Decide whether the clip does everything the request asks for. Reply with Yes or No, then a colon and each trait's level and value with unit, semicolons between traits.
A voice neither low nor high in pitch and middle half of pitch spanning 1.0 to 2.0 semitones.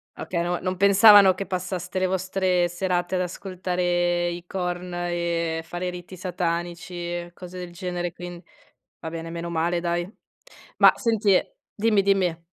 Yes: medium, 175 Hz; narrow, 1.3 semitones